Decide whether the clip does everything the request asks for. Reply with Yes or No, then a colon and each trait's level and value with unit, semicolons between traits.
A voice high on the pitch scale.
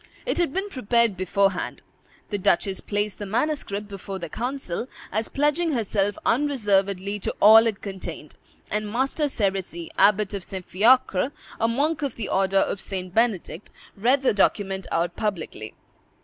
Yes: high, 205 Hz